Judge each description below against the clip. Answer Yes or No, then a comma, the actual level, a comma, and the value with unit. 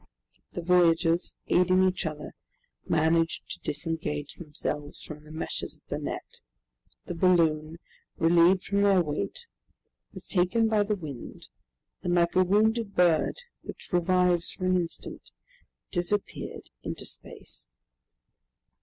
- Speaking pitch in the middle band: Yes, medium, 175 Hz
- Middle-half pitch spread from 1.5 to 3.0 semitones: Yes, narrow, 2.4 semitones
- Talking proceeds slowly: Yes, slow, 125 wpm